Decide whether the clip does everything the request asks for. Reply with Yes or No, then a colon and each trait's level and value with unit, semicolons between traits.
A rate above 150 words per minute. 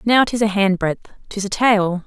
Yes: fast, 205 wpm